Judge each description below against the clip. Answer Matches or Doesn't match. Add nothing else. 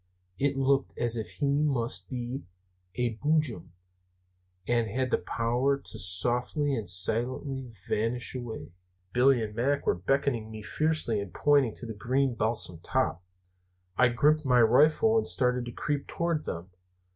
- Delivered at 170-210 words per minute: Doesn't match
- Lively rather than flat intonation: Doesn't match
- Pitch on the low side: Matches